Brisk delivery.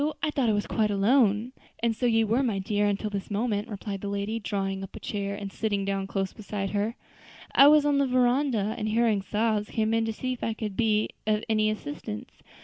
Yes: fast, 225 wpm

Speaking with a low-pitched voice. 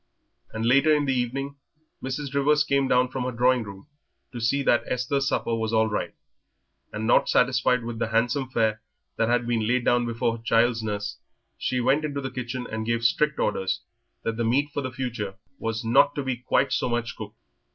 Yes: low, 125 Hz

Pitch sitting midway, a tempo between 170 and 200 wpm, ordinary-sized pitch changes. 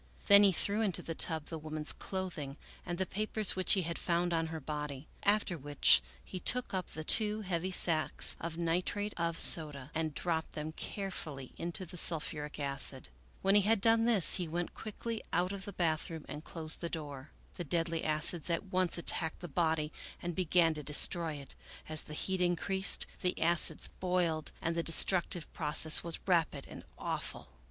Yes: medium, 170 Hz; average, 185 wpm; average, 3.1 semitones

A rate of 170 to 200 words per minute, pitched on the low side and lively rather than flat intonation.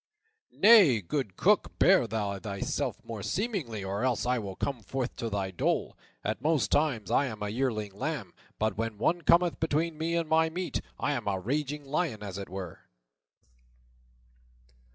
Yes: average, 175 wpm; low, 120 Hz; wide, 7.5 semitones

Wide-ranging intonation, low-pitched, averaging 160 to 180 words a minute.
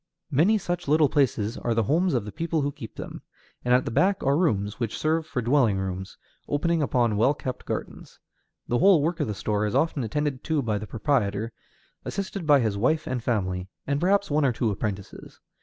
No: wide, 6.4 semitones; low, 130 Hz; fast, 205 wpm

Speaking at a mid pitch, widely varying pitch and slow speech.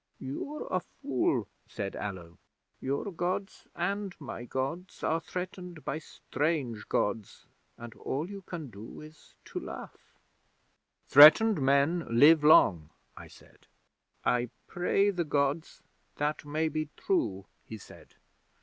Yes: medium, 150 Hz; wide, 6.2 semitones; slow, 125 wpm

